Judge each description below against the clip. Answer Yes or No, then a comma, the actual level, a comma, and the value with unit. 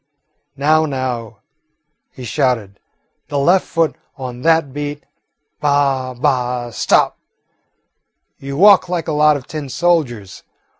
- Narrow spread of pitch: No, average, 3.7 semitones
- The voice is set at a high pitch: No, medium, 140 Hz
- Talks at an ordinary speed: No, slow, 120 wpm